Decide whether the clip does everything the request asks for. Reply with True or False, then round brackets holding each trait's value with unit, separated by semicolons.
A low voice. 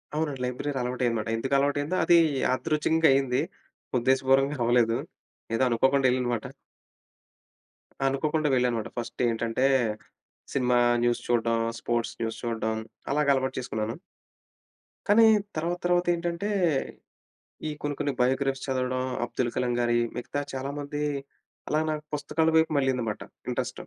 True (130 Hz)